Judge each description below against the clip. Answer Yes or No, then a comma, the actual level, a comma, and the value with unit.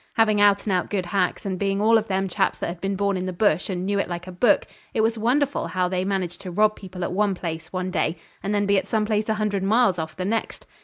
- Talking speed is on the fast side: Yes, fast, 285 wpm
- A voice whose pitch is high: Yes, high, 195 Hz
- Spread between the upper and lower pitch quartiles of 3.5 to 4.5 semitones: No, narrow, 2.5 semitones